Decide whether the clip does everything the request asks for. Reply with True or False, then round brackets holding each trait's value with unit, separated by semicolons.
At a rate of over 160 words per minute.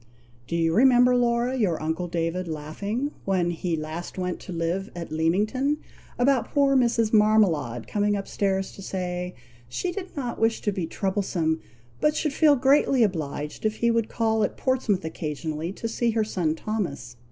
True (170 wpm)